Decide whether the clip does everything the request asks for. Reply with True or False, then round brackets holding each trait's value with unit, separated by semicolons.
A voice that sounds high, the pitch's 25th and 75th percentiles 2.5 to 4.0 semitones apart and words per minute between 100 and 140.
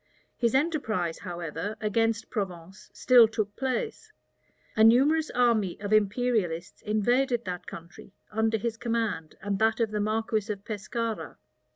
True (220 Hz; 2.9 semitones; 135 wpm)